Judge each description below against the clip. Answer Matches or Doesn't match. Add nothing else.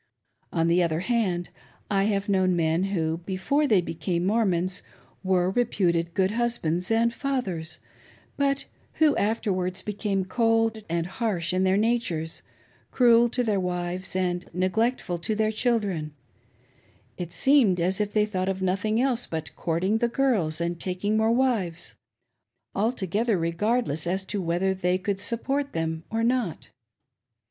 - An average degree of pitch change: Matches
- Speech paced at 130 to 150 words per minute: Matches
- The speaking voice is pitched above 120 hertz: Matches